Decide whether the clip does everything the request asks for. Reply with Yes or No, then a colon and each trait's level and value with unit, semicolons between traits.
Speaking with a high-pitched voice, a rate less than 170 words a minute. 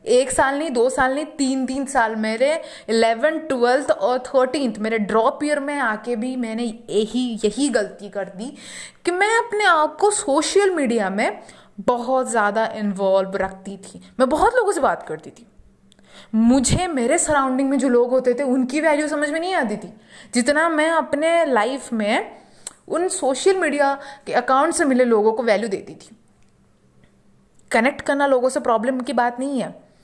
No: very high, 260 Hz; average, 175 wpm